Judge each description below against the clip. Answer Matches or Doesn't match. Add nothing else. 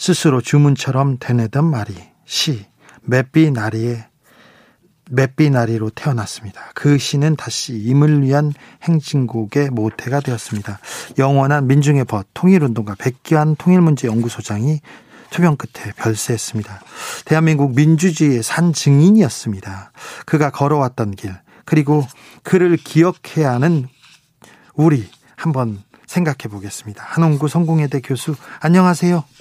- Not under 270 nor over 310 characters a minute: Matches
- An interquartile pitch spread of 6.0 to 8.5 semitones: Doesn't match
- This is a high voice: Doesn't match